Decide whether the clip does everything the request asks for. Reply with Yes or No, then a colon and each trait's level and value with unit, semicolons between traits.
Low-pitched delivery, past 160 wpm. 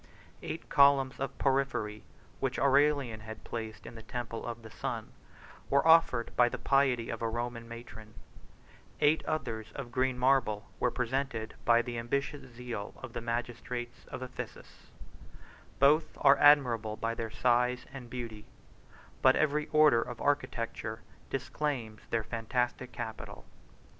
No: low, 120 Hz; average, 140 wpm